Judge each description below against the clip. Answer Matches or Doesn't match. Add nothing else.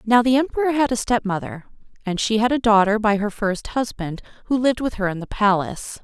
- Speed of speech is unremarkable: Doesn't match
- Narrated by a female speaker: Matches